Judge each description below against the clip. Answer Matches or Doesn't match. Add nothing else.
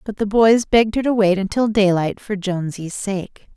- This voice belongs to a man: Doesn't match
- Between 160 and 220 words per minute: Matches